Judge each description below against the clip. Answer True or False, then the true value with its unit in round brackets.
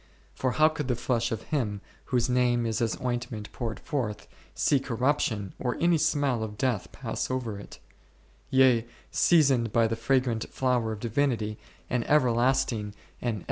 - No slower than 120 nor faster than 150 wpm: False (170 wpm)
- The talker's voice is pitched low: True (120 Hz)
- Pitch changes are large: False (2.8 semitones)